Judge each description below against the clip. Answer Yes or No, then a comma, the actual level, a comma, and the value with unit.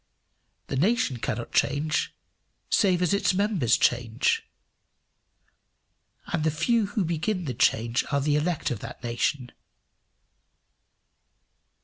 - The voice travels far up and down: Yes, wide, 7.0 semitones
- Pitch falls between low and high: Yes, medium, 155 Hz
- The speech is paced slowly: Yes, slow, 110 wpm